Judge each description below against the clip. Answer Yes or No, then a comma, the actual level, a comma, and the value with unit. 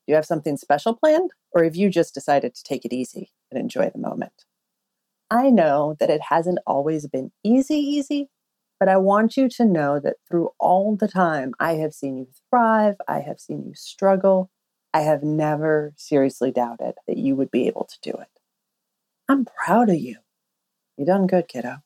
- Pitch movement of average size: No, wide, 6.9 semitones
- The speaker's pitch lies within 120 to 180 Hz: No, high, 190 Hz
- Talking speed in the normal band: Yes, average, 190 wpm